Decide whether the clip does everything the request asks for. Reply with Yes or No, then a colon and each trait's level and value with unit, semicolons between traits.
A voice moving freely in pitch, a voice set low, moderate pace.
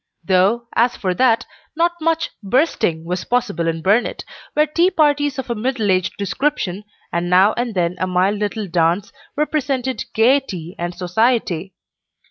No: wide, 6.4 semitones; high, 210 Hz; average, 150 wpm